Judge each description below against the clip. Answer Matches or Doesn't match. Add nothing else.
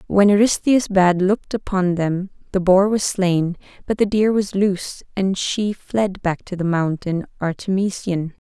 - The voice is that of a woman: Matches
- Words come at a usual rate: Matches